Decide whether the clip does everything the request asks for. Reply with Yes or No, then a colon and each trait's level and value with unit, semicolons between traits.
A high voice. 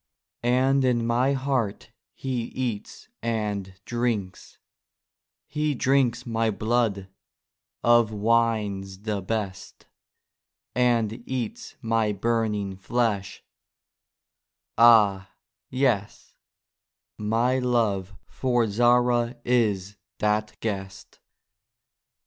No: low, 115 Hz